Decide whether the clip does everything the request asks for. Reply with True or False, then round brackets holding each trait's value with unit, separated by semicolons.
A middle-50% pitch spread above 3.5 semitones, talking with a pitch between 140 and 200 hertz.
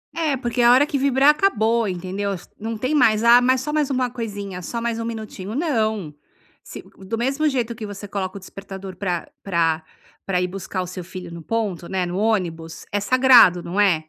False (4.8 semitones; 215 Hz)